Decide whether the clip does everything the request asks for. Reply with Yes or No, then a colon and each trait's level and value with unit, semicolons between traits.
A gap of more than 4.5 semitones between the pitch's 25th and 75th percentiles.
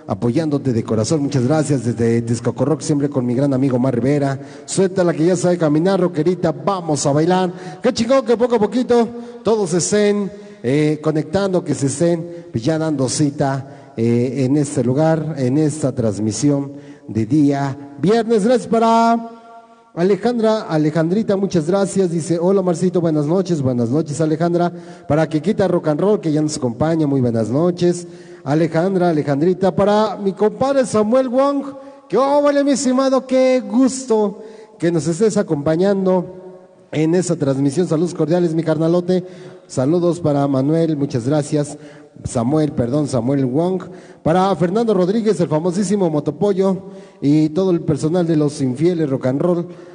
Yes: average, 5.0 semitones